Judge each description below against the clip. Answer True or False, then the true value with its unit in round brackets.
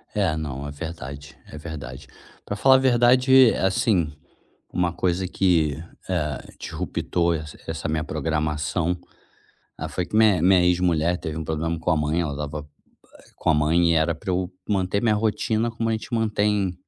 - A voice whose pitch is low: True (85 Hz)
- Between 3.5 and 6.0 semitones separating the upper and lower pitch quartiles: True (4.9 semitones)